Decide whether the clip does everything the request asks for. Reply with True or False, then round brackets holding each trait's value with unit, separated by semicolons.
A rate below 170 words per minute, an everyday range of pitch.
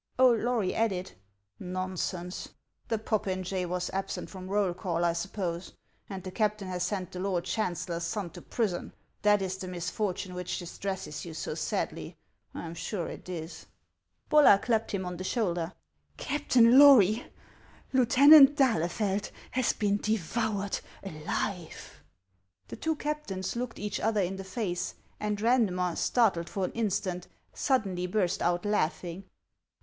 True (150 wpm; 3.5 semitones)